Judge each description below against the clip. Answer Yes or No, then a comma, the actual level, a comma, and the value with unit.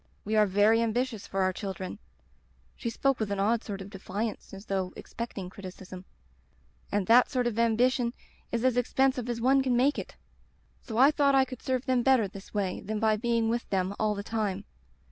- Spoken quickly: Yes, fast, 210 wpm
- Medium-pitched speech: No, high, 220 Hz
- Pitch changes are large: No, average, 3.9 semitones